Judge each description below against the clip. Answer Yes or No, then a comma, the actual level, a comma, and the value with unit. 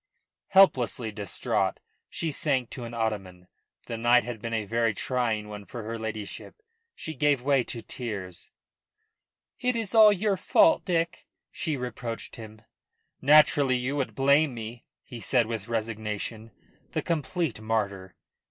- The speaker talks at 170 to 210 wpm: No, average, 145 wpm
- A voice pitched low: Yes, low, 120 Hz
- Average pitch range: Yes, average, 4.7 semitones